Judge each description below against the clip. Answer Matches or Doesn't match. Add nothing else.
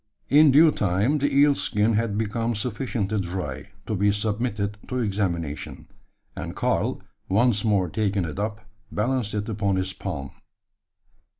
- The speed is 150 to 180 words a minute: Doesn't match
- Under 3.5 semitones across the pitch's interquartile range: Matches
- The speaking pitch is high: Doesn't match